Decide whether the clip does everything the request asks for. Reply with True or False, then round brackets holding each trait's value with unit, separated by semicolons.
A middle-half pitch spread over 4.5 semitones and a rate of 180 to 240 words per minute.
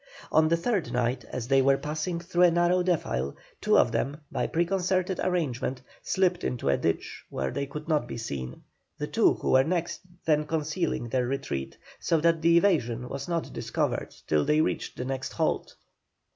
True (5.5 semitones; 185 wpm)